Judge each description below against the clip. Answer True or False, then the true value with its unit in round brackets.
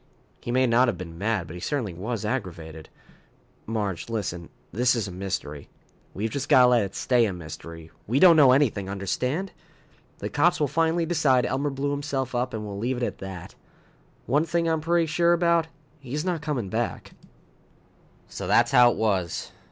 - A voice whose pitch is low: True (125 Hz)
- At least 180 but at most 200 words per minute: True (185 wpm)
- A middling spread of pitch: False (7.0 semitones)